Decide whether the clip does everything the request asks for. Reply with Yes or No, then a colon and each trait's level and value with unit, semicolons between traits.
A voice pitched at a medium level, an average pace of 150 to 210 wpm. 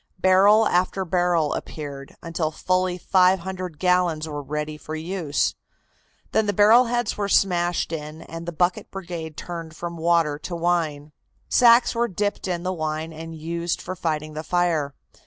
Yes: medium, 170 Hz; average, 160 wpm